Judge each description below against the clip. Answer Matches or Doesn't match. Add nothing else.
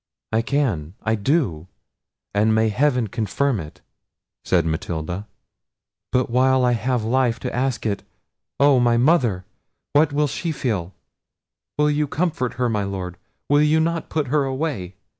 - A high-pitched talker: Doesn't match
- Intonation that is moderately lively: Doesn't match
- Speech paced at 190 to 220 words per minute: Doesn't match